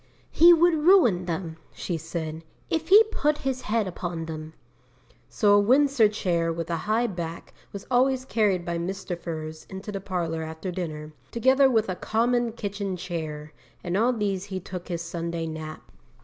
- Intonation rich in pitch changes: Yes, wide, 5.7 semitones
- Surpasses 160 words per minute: Yes, average, 170 wpm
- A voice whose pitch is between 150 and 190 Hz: Yes, medium, 185 Hz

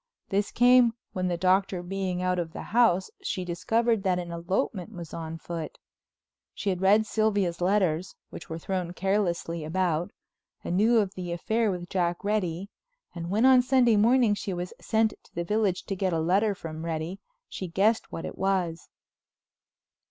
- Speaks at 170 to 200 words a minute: Yes, average, 175 wpm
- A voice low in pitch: No, medium, 185 Hz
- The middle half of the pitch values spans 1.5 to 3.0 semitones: No, average, 3.4 semitones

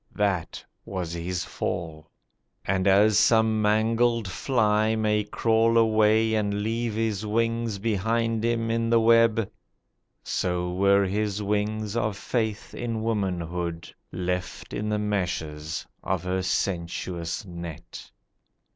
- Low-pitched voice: Yes, low, 105 Hz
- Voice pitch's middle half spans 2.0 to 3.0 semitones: No, average, 3.5 semitones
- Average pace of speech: No, slow, 120 wpm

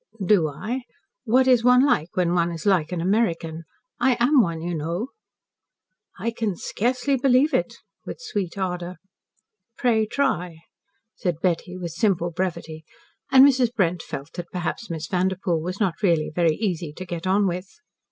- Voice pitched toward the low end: No, medium, 185 Hz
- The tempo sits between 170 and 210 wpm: No, average, 160 wpm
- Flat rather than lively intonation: No, average, 5.3 semitones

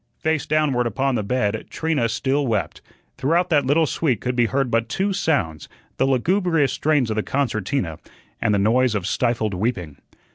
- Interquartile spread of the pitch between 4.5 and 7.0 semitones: Yes, average, 5.1 semitones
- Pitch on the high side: No, low, 125 Hz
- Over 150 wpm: Yes, average, 175 wpm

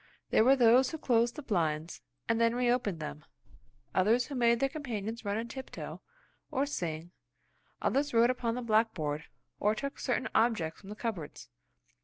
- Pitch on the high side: Yes, high, 230 Hz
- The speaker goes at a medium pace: Yes, average, 165 wpm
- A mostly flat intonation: No, average, 4.0 semitones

